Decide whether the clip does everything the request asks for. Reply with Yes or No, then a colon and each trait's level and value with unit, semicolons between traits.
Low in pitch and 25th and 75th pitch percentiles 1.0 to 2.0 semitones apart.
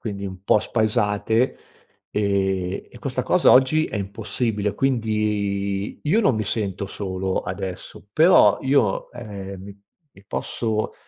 No: low, 105 Hz; narrow, 2.5 semitones